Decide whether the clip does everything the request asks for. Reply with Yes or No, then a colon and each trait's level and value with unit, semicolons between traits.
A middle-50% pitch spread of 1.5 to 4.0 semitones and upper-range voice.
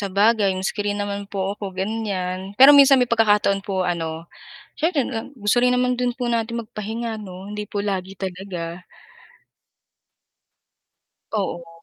Yes: average, 3.4 semitones; high, 205 Hz